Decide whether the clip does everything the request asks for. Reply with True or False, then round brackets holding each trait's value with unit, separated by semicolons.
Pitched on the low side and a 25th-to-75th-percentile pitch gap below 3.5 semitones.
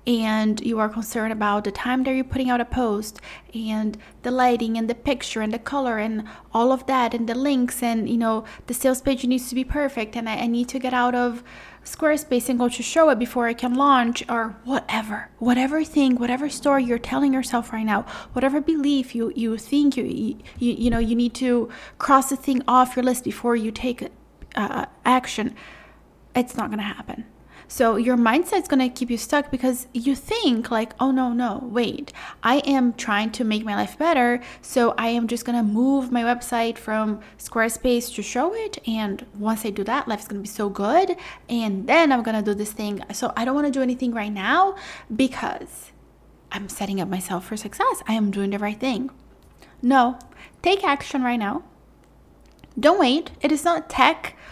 False (245 Hz; 2.9 semitones)